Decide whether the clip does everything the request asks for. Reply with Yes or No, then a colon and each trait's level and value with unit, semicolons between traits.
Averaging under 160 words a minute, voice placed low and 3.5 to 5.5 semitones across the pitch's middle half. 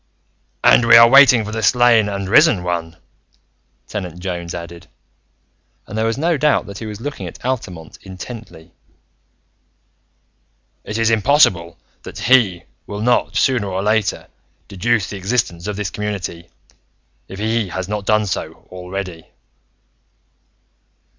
Yes: slow, 135 wpm; low, 105 Hz; average, 4.1 semitones